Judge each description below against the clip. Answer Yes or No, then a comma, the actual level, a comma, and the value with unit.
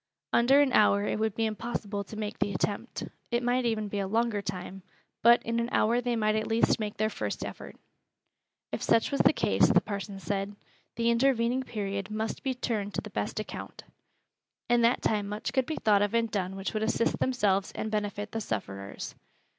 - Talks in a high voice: Yes, high, 215 Hz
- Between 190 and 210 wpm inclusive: Yes, average, 200 wpm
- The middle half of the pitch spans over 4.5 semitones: No, narrow, 2.5 semitones